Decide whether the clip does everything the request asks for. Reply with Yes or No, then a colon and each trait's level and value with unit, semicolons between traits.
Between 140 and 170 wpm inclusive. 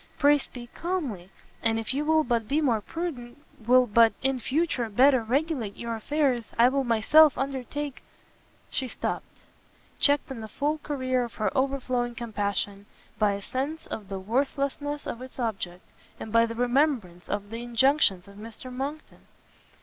Yes: average, 165 wpm